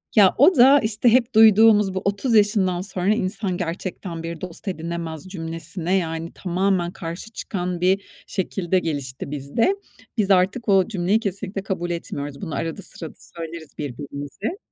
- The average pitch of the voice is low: No, medium, 185 Hz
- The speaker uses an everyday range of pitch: Yes, average, 3.6 semitones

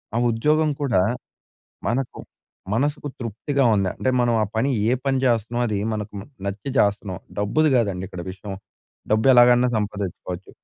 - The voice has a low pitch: Yes, low, 115 Hz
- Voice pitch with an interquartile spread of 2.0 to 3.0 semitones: No, average, 4.3 semitones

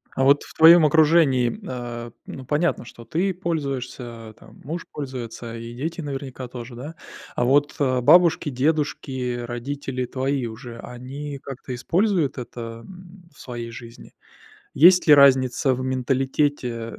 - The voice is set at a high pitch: No, low, 135 Hz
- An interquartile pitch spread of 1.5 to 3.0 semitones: No, average, 3.6 semitones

